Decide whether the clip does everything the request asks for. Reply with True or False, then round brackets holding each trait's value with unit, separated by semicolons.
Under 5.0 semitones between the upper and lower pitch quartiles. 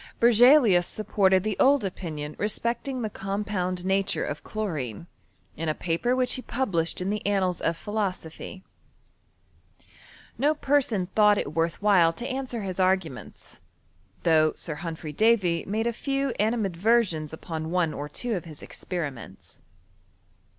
False (5.3 semitones)